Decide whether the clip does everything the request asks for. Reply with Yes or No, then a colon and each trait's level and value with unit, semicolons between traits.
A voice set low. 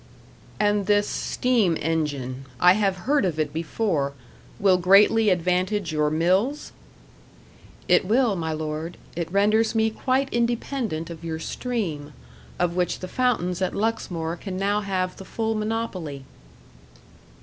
No: medium, 185 Hz